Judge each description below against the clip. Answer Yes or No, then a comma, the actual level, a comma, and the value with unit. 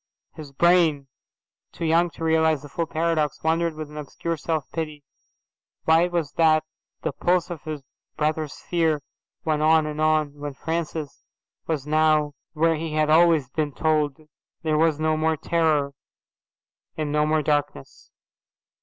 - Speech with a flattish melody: Yes, narrow, 1.4 semitones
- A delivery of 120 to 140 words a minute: No, average, 155 wpm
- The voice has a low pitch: No, medium, 155 Hz